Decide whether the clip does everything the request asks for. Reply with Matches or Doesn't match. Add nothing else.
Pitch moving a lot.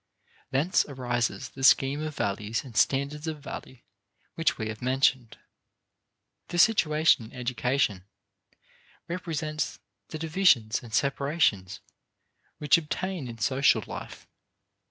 Doesn't match